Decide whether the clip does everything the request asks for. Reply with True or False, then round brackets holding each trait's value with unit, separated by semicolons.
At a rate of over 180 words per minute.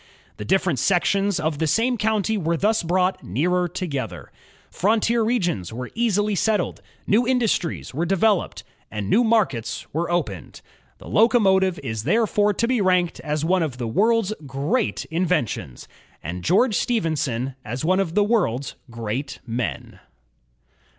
False (140 wpm)